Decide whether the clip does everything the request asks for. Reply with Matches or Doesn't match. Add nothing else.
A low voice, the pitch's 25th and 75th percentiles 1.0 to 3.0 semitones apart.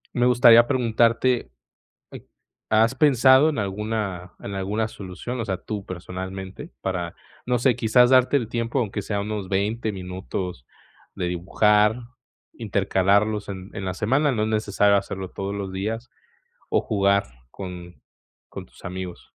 Doesn't match